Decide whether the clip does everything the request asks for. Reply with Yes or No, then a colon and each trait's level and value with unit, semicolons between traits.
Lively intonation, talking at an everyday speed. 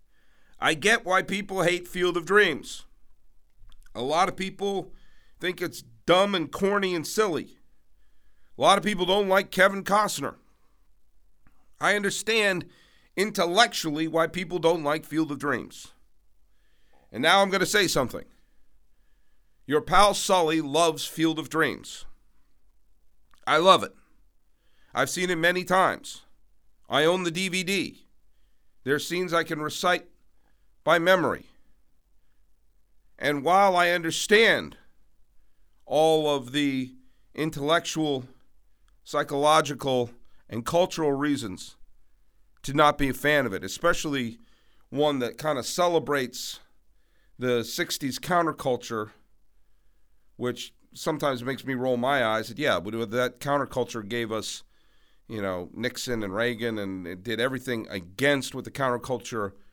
No: wide, 6.5 semitones; slow, 125 wpm